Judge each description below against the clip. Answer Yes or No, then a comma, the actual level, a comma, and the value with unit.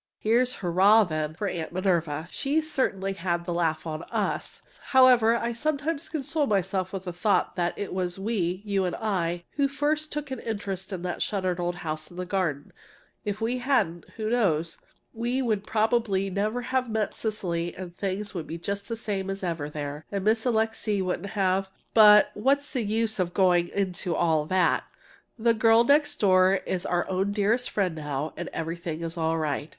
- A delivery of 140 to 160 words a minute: No, average, 185 wpm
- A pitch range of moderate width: Yes, average, 4.5 semitones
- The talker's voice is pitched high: Yes, high, 195 Hz